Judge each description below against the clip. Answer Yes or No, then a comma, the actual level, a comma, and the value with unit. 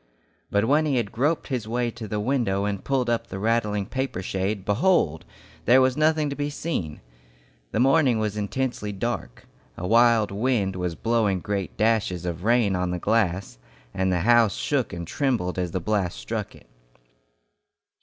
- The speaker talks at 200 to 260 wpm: No, average, 175 wpm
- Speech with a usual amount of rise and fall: Yes, average, 4.5 semitones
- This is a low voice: Yes, low, 110 Hz